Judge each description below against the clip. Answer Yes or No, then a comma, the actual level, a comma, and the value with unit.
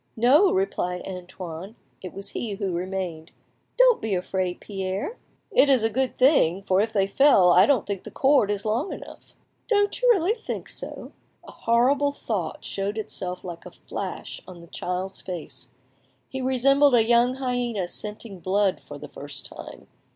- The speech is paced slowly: No, average, 170 wpm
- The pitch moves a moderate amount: No, wide, 6.2 semitones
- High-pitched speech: Yes, high, 210 Hz